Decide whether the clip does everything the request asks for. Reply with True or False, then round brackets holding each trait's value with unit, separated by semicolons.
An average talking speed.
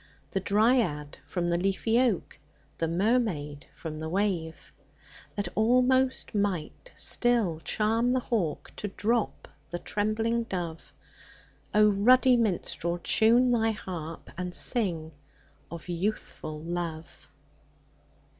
False (110 wpm)